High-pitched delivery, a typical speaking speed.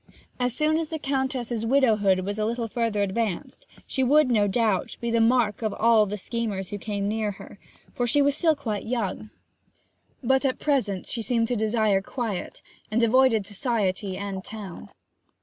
Yes: high, 225 Hz; average, 175 wpm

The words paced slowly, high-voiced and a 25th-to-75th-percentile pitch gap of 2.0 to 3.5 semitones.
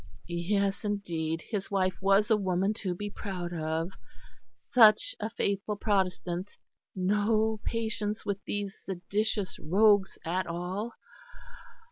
Yes: slow, 115 wpm; high, 200 Hz; average, 2.7 semitones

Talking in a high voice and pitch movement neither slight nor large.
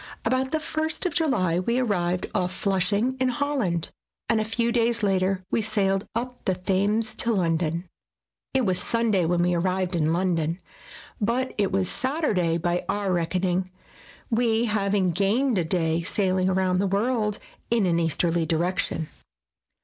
Yes: high, 195 Hz; average, 4.6 semitones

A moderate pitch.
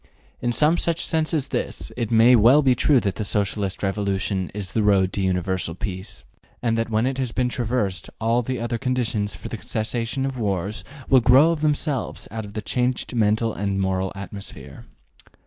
No: low, 115 Hz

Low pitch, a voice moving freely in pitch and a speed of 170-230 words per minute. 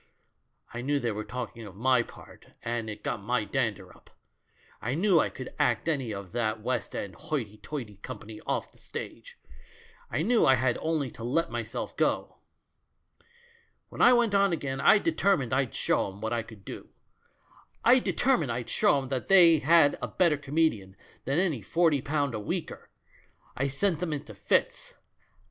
Yes: low, 130 Hz; wide, 6.0 semitones; average, 175 wpm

